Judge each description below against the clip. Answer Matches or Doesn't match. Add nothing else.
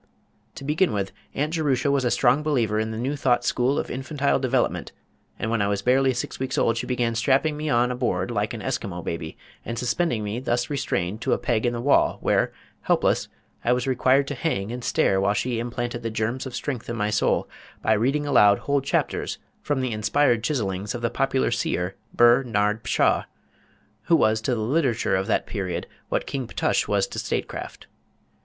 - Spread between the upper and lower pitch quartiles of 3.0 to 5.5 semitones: Matches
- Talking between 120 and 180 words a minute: Doesn't match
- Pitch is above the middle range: Doesn't match